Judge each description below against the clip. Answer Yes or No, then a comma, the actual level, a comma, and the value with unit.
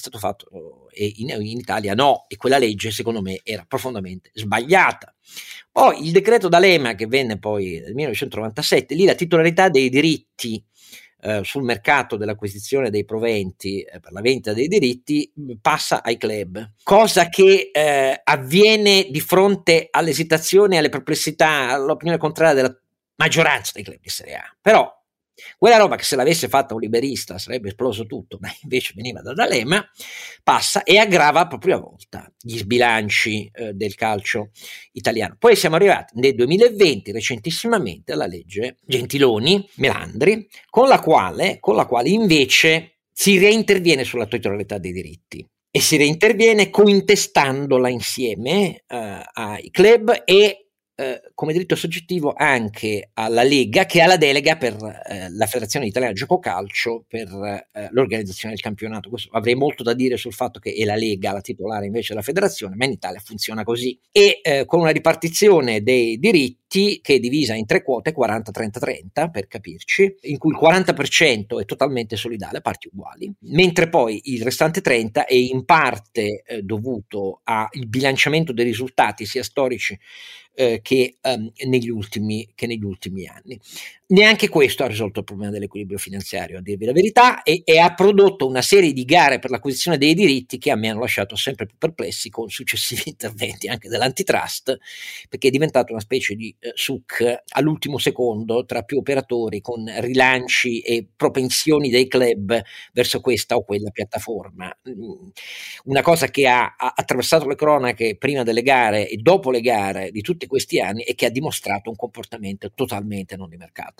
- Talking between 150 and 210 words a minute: Yes, average, 160 wpm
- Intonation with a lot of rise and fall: Yes, wide, 6.6 semitones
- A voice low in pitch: Yes, low, 125 Hz